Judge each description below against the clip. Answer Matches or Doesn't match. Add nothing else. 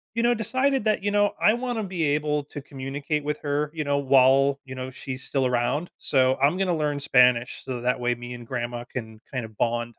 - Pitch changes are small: Doesn't match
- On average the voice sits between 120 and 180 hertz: Matches